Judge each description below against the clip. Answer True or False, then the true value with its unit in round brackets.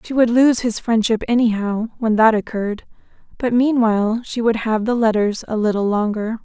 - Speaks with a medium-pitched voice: False (225 Hz)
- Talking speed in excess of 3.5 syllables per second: True (5.2 syllables/s)